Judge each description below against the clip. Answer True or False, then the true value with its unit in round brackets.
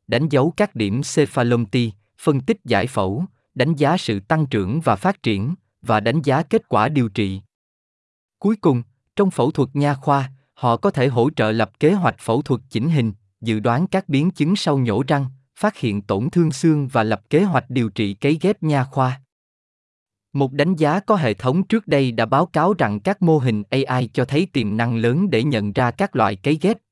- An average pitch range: False (5.7 semitones)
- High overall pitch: False (135 Hz)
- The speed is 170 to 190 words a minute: False (210 wpm)